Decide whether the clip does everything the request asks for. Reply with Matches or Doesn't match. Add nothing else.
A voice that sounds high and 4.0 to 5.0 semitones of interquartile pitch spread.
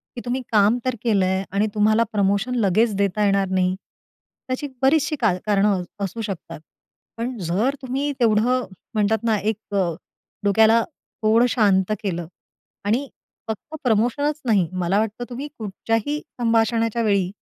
Doesn't match